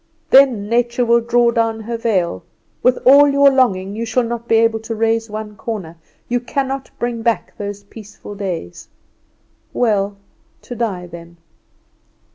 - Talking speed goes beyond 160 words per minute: No, average, 150 wpm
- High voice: Yes, high, 225 Hz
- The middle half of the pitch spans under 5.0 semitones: Yes, average, 2.8 semitones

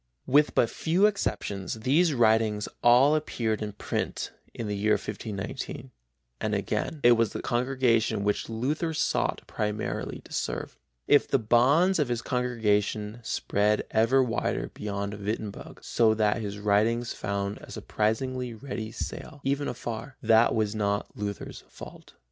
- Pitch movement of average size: Yes, average, 3.6 semitones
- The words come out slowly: No, average, 145 wpm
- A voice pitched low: Yes, low, 115 Hz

